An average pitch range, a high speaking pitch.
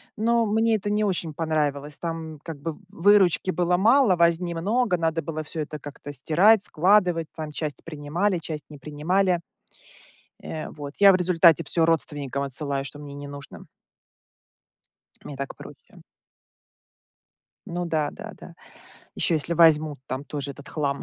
No: average, 3.6 semitones; medium, 165 Hz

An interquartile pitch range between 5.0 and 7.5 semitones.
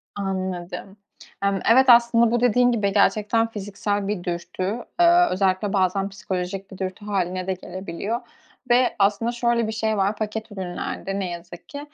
No: average, 3.3 semitones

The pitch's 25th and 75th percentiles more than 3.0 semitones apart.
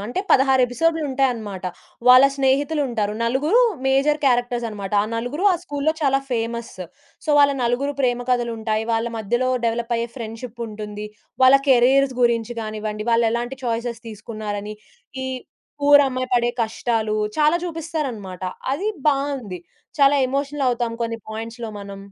Yes: average, 3.5 semitones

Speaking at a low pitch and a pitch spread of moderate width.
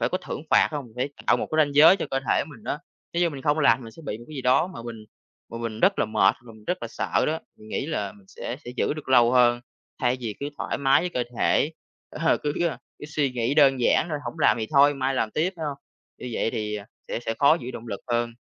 Yes: low, 130 Hz; average, 4.4 semitones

